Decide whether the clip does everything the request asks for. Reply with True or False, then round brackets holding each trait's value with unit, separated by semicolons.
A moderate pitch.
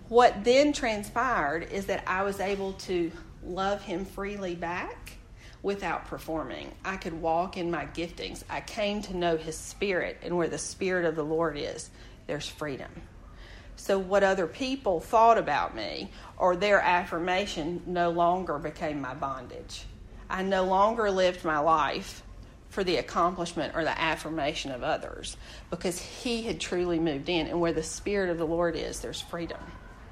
True (175 Hz)